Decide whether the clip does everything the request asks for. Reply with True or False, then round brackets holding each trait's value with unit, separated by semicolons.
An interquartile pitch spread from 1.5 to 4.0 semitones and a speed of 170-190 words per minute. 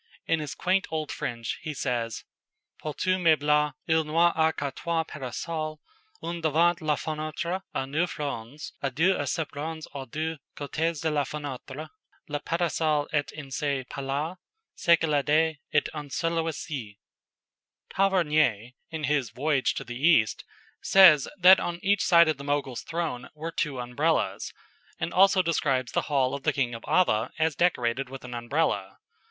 True (3.2 semitones; 175 wpm)